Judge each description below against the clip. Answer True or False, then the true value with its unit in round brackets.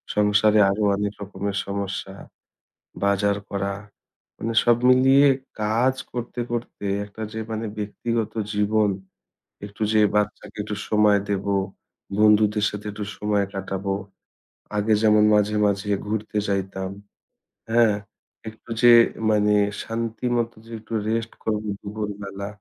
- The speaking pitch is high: False (105 Hz)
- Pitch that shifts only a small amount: True (1.5 semitones)